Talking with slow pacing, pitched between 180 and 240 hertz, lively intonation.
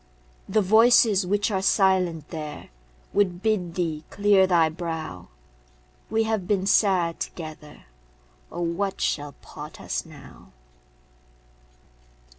No: slow, 110 wpm; medium, 185 Hz; average, 3.7 semitones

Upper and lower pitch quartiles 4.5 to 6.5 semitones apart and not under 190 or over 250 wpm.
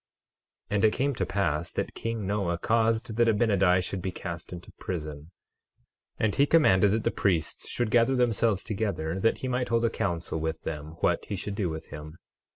Yes: average, 5.0 semitones; average, 195 wpm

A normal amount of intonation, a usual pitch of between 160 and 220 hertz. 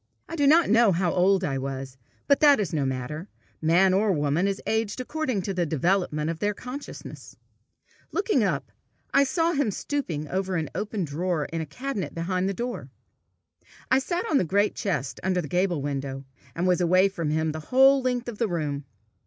No: wide, 7.2 semitones; medium, 185 Hz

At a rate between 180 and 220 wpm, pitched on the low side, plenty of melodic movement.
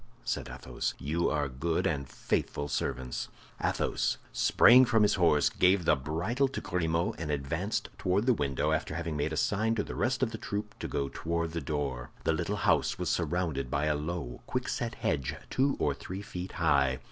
Yes: average, 190 wpm; very low, 85 Hz; wide, 5.9 semitones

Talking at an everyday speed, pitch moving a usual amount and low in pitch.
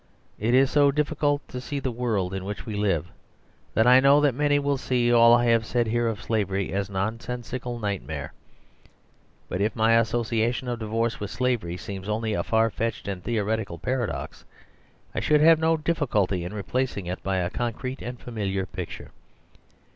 Yes: average, 185 wpm; average, 4.1 semitones; low, 115 Hz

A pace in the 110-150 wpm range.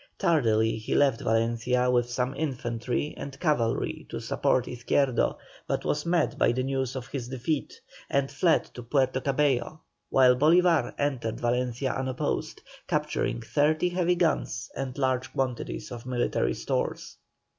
Yes: average, 140 wpm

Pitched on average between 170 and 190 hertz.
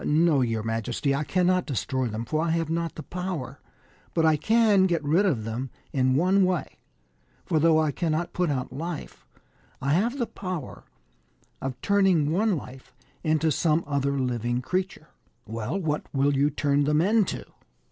No: medium, 155 Hz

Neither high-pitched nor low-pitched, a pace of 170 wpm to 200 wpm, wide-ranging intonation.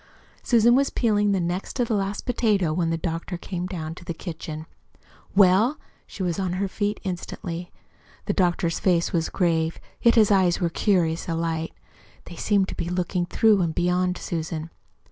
No: medium, 180 Hz; average, 175 wpm; average, 3.1 semitones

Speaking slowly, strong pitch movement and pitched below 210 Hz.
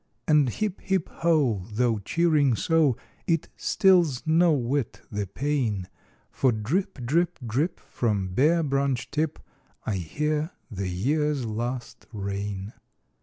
Yes: slow, 120 wpm; wide, 6.5 semitones; low, 135 Hz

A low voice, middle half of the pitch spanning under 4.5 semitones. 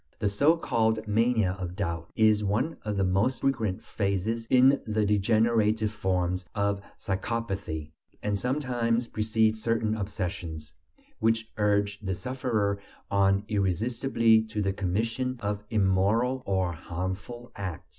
Yes: low, 105 Hz; average, 2.8 semitones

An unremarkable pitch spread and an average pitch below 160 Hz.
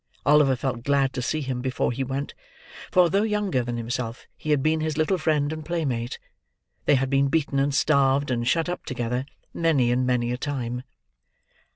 Yes: average, 3.8 semitones; low, 135 Hz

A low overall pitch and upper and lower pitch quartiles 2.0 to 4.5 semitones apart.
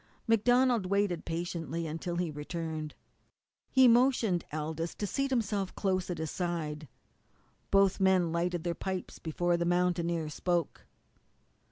No: medium, 175 Hz; average, 3.1 semitones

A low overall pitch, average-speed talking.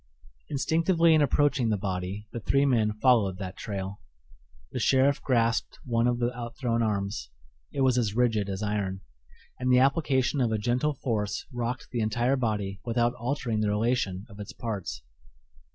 Yes: low, 115 Hz; average, 165 wpm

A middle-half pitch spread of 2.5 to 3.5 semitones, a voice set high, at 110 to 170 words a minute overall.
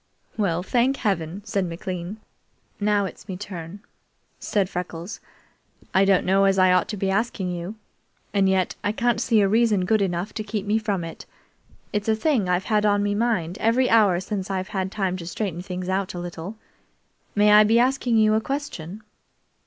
No: average, 2.9 semitones; high, 200 Hz; average, 190 wpm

